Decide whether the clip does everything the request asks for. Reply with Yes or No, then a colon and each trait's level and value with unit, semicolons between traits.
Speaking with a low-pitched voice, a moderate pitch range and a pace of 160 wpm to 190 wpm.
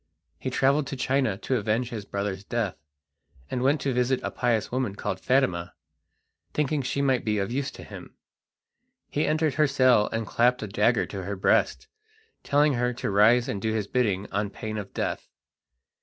Yes: low, 120 Hz; average, 4.4 semitones; average, 185 wpm